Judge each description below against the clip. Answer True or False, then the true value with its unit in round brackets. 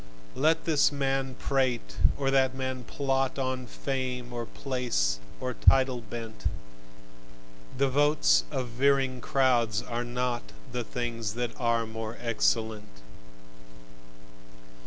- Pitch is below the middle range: True (125 Hz)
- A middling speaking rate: False (115 wpm)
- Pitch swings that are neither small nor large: False (2.3 semitones)